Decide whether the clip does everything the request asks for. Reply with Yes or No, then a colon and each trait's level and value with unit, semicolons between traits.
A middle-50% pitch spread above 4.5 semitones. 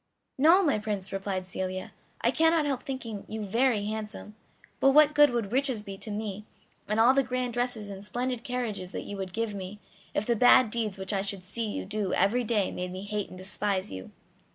No: average, 4.0 semitones